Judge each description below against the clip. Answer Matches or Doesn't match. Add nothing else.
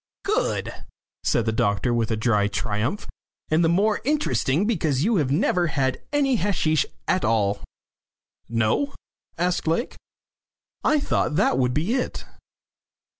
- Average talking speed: Doesn't match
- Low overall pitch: Doesn't match